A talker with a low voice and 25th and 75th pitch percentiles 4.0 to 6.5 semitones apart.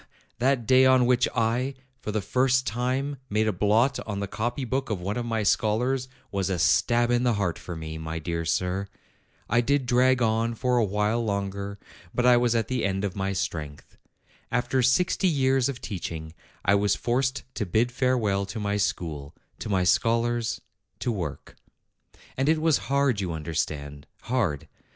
Yes: low, 115 Hz; average, 4.5 semitones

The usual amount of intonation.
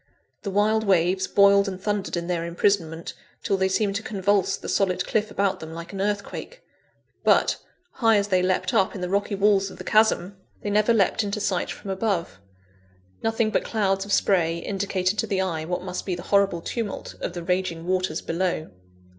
No: narrow, 2.1 semitones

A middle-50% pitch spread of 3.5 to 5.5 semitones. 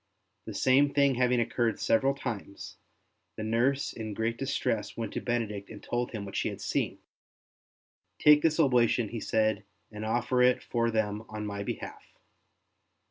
No: average, 2.7 semitones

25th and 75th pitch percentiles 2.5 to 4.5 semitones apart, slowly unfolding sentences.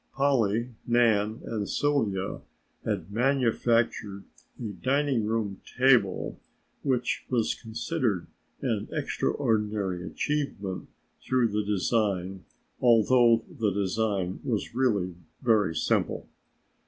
Yes: average, 3.7 semitones; slow, 80 wpm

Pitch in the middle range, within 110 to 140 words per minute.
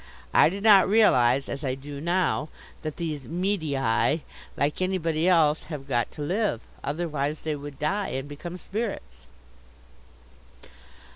Yes: medium, 155 Hz; slow, 135 wpm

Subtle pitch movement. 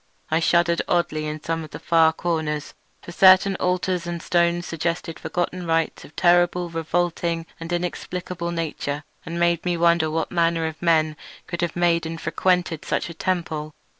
Yes: narrow, 1.3 semitones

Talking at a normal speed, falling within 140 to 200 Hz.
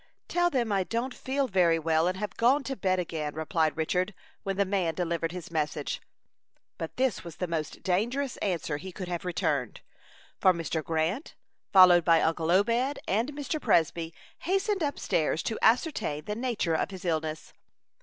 Yes: average, 175 wpm; medium, 185 Hz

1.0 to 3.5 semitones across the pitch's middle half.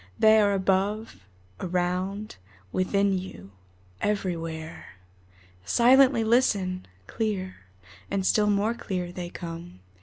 Yes: average, 2.9 semitones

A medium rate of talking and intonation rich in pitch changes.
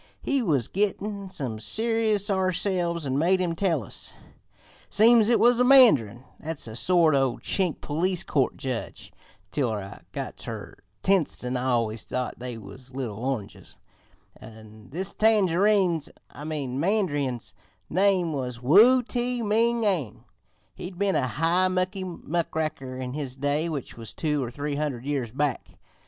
Yes: average, 150 wpm; wide, 7.2 semitones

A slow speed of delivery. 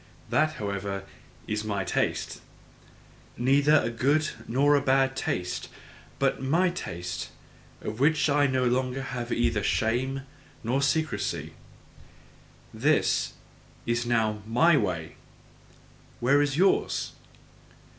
Yes: slow, 110 wpm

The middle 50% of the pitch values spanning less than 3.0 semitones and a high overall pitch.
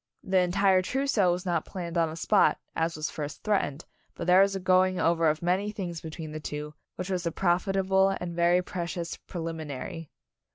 No: narrow, 2.5 semitones; medium, 175 Hz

